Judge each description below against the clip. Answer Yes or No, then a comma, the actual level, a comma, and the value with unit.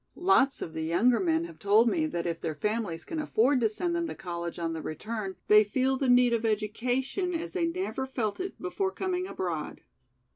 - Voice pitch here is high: Yes, high, 240 Hz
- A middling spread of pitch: No, wide, 8.7 semitones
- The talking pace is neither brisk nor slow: No, fast, 210 wpm